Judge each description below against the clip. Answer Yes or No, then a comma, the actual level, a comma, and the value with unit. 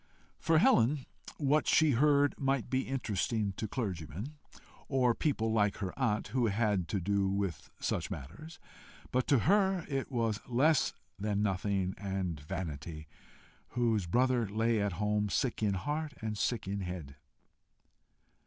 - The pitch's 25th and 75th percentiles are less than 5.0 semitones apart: No, average, 5.3 semitones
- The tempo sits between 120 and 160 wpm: Yes, average, 145 wpm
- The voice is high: No, low, 110 Hz